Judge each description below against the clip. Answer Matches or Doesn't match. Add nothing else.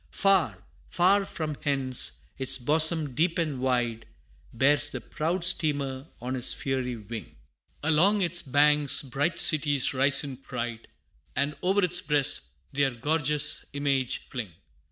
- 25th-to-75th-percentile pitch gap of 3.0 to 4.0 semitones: Matches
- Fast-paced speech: Doesn't match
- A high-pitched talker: Doesn't match